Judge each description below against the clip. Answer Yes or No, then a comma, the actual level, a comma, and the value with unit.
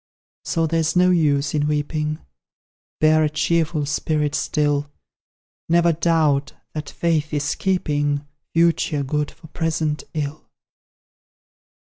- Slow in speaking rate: Yes, slow, 110 wpm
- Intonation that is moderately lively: No, narrow, 1.9 semitones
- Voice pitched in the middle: Yes, medium, 155 Hz